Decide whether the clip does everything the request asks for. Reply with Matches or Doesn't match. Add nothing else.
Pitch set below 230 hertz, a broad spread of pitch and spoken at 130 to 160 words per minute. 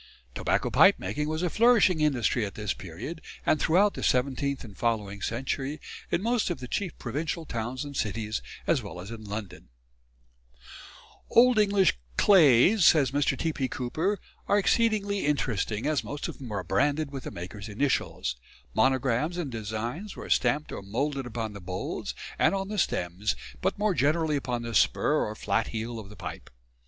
Doesn't match